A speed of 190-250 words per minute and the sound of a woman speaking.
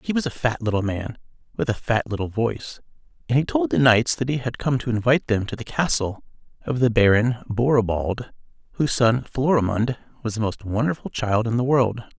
No: average, 200 wpm; male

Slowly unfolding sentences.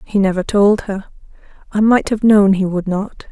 No: average, 200 wpm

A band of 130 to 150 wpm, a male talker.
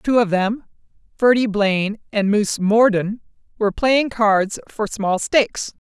No: average, 145 wpm; female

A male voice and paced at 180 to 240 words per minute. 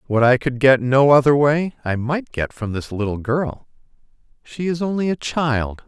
Yes: male; average, 195 wpm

